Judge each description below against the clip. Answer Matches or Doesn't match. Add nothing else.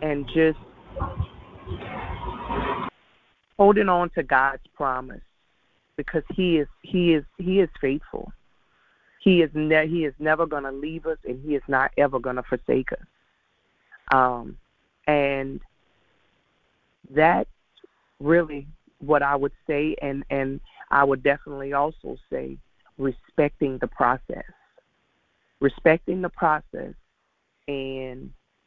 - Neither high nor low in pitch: Matches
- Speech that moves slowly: Matches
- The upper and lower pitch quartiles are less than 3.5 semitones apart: Matches